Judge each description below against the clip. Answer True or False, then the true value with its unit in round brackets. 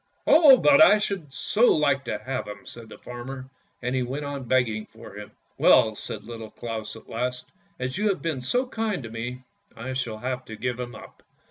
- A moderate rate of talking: False (225 wpm)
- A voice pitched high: False (125 Hz)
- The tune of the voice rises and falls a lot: False (4.4 semitones)